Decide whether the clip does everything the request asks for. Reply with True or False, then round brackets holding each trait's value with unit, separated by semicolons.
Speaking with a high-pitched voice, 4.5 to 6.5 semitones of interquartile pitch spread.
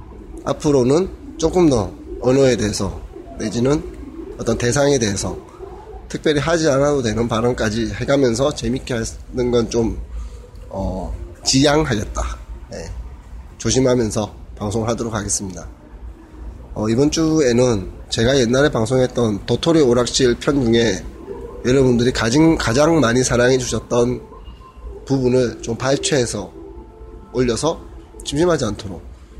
False (120 Hz; 5.2 semitones)